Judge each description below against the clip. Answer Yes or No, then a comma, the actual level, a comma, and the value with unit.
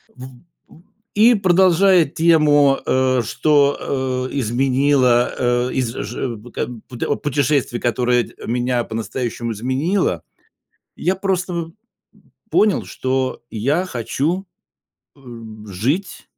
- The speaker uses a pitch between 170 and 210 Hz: No, low, 130 Hz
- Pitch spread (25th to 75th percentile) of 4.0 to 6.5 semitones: Yes, average, 5.1 semitones